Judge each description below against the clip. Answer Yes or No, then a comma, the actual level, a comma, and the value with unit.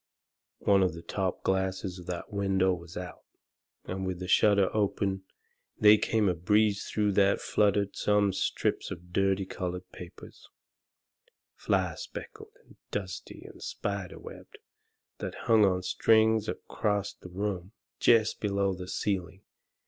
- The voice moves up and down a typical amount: No, narrow, 2.1 semitones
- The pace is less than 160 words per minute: Yes, average, 140 wpm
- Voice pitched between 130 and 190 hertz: No, very low, 95 Hz